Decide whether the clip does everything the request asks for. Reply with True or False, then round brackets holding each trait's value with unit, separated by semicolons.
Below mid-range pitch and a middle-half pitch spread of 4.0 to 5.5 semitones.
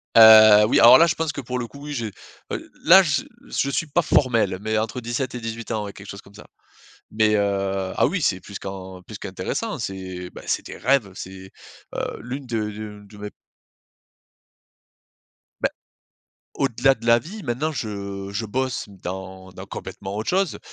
True (110 Hz; 4.3 semitones)